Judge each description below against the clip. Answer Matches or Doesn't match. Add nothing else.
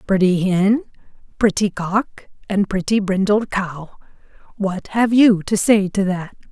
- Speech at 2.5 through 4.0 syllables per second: Matches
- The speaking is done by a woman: Matches